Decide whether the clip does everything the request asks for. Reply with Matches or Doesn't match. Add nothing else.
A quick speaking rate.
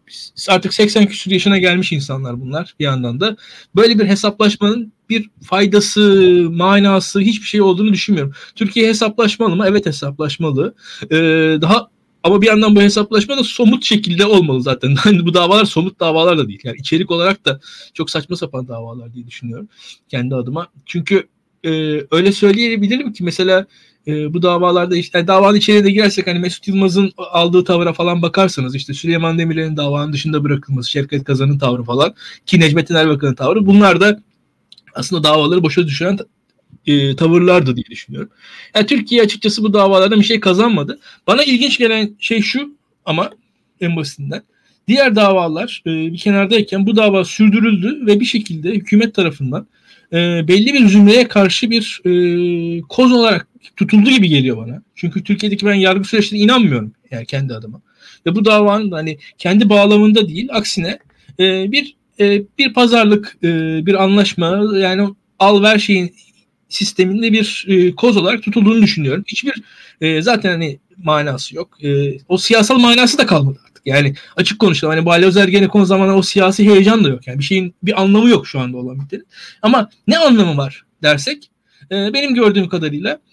Matches